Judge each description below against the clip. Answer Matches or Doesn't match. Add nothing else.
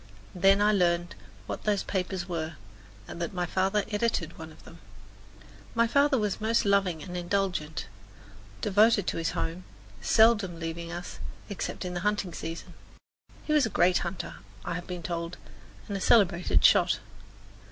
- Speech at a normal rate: Matches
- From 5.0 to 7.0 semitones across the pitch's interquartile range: Doesn't match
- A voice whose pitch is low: Doesn't match